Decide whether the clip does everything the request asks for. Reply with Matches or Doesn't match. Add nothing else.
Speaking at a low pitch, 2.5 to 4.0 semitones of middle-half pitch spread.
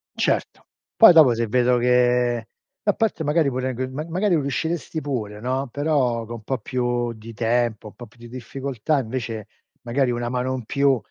Matches